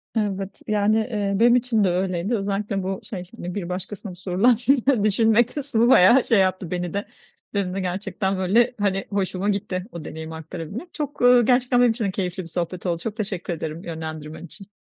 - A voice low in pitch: No, high, 195 Hz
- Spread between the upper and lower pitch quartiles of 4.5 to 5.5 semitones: No, average, 3.6 semitones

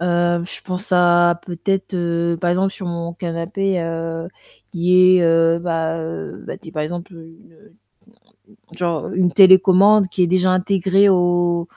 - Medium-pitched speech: Yes, medium, 175 Hz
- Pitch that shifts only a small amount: Yes, narrow, 1.7 semitones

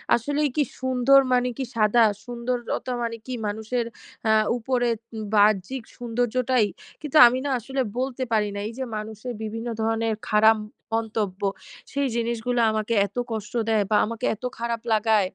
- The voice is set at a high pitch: Yes, high, 230 Hz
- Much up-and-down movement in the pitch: No, narrow, 2.5 semitones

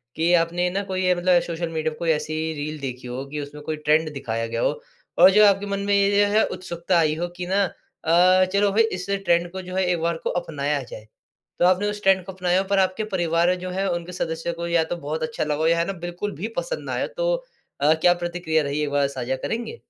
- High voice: No, medium, 175 Hz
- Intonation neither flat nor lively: Yes, average, 3.2 semitones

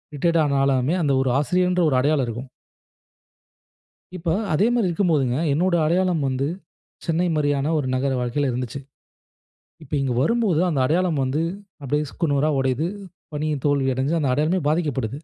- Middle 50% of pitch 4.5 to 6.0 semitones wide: No, average, 3.8 semitones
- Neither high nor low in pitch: Yes, medium, 145 Hz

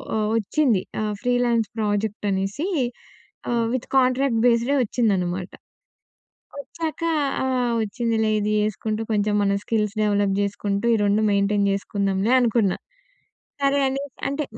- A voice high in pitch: Yes, high, 215 Hz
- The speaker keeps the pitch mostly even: No, average, 3.4 semitones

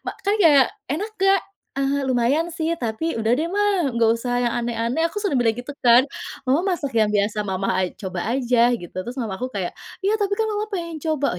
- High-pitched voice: Yes, very high, 265 Hz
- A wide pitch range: Yes, wide, 6.7 semitones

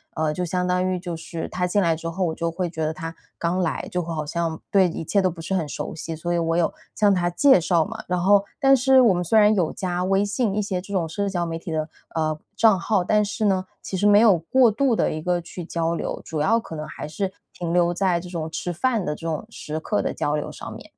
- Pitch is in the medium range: Yes, medium, 180 Hz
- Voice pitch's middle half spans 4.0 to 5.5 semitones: No, average, 3.4 semitones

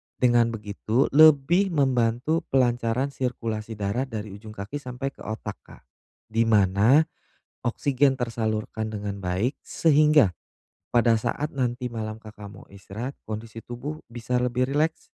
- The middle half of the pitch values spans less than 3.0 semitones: No, average, 3.8 semitones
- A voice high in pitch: No, low, 120 Hz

